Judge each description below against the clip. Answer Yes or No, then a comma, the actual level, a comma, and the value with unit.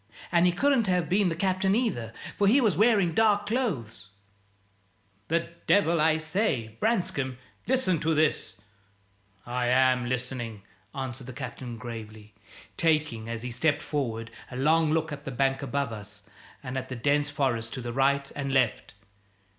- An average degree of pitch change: No, wide, 6.3 semitones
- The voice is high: No, low, 135 Hz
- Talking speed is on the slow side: No, average, 160 wpm